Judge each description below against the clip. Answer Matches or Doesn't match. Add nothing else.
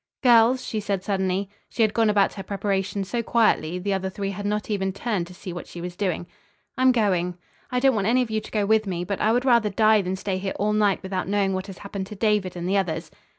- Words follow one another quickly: Matches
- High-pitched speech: Matches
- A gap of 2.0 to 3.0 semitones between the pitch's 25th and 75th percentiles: Matches